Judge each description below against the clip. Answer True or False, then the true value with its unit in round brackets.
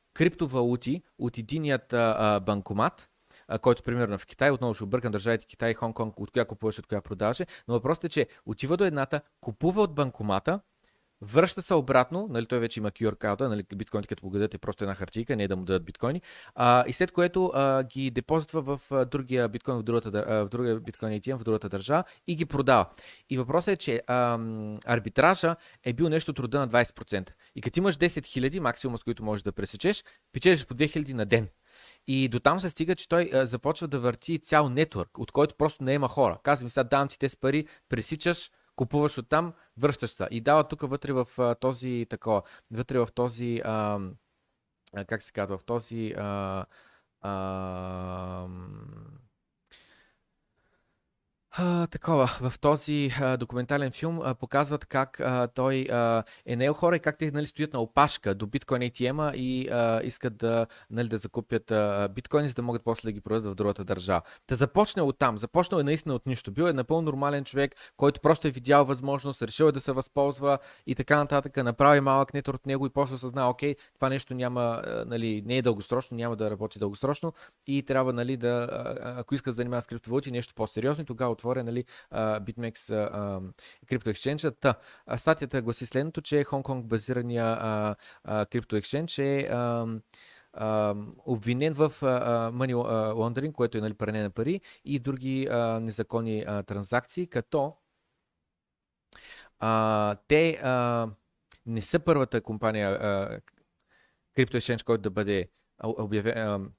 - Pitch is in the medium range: False (125 Hz)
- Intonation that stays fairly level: False (4.3 semitones)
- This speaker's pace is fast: True (170 wpm)